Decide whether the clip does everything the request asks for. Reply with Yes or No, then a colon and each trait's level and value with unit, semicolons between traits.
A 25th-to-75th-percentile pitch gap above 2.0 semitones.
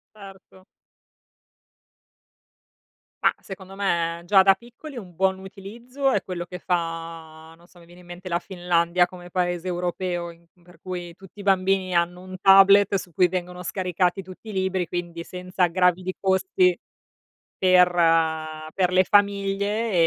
No: narrow, 1.7 semitones